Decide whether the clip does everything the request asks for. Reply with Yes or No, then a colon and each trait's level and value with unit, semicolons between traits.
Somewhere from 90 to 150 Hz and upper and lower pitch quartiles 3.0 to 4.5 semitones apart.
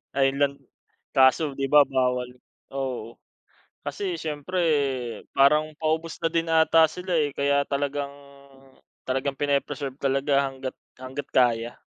No: medium, 140 Hz; narrow, 2.6 semitones